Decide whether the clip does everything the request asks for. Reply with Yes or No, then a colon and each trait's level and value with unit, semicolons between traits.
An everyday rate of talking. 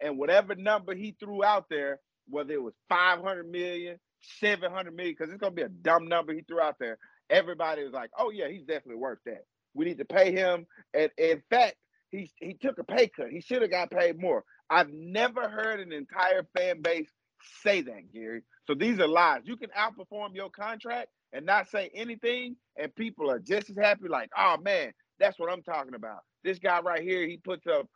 No: fast, 215 wpm